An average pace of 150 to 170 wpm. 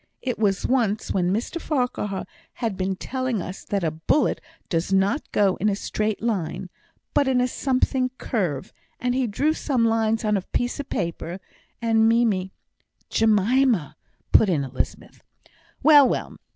Yes: average, 160 wpm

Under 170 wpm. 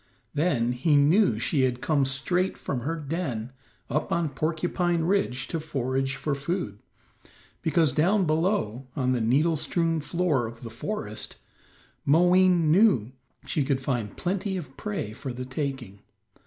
Yes: average, 145 wpm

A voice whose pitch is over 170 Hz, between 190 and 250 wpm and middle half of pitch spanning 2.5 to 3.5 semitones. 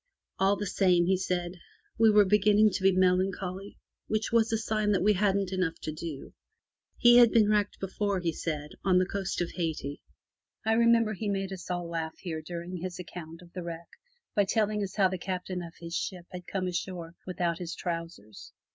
Yes: medium, 185 Hz; average, 200 wpm; average, 2.9 semitones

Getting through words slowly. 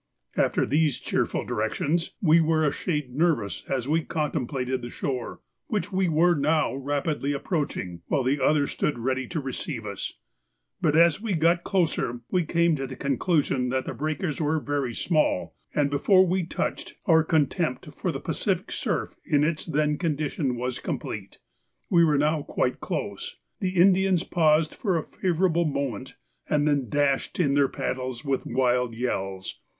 No: average, 165 wpm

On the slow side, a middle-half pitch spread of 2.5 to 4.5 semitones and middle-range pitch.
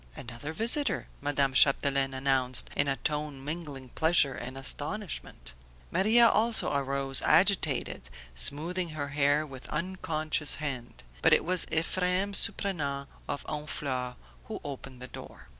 Yes: slow, 125 wpm; average, 3.9 semitones; medium, 145 Hz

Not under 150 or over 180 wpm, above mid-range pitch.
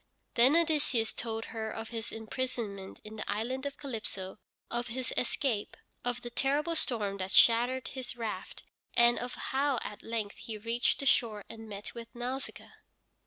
Yes: average, 165 wpm; high, 235 Hz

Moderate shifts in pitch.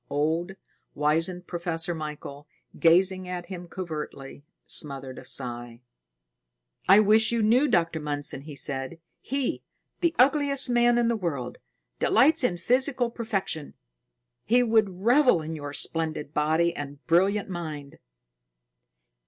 No: wide, 6.8 semitones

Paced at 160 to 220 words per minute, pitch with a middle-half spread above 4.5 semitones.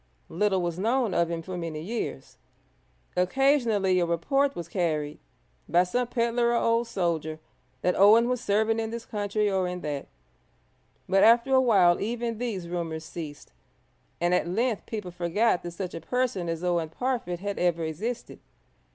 Yes: average, 165 wpm; average, 5.2 semitones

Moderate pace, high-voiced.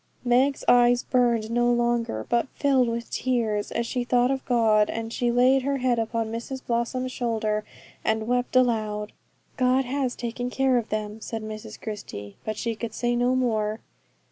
Yes: average, 170 wpm; high, 240 Hz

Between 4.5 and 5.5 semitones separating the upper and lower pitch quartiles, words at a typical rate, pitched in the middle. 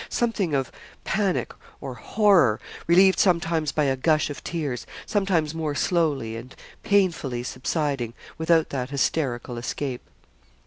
No: average, 4.9 semitones; slow, 125 wpm; medium, 150 Hz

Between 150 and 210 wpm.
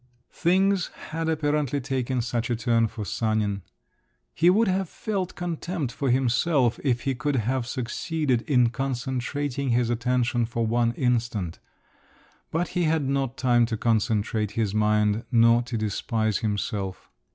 No: average, 140 wpm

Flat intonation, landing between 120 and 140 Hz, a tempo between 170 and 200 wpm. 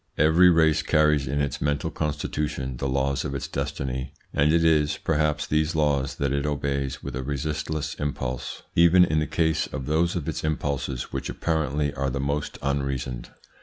No: narrow, 2.2 semitones; very low, 75 Hz; average, 175 wpm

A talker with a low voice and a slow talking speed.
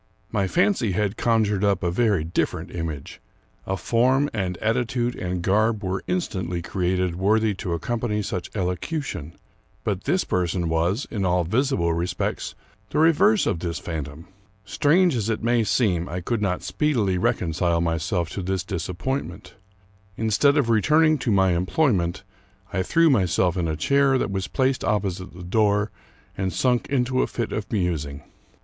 No: low, 100 Hz; average, 160 wpm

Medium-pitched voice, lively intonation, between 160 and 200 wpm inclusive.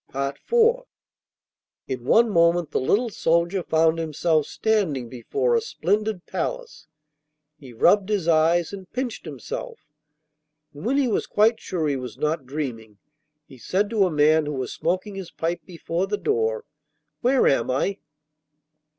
No: medium, 170 Hz; wide, 6.3 semitones; average, 150 wpm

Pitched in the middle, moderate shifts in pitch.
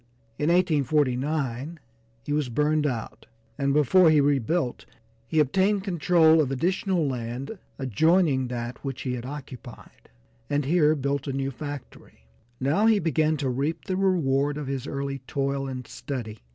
Yes: medium, 145 Hz; average, 3.2 semitones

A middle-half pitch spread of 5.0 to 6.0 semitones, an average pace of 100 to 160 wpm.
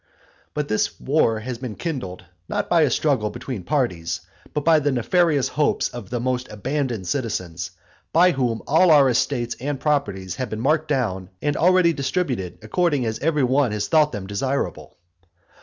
No: wide, 5.6 semitones; average, 170 wpm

